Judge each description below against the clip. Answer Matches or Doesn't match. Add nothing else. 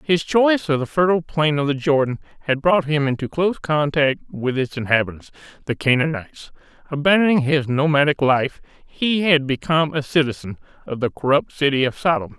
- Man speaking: Matches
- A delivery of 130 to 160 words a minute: Doesn't match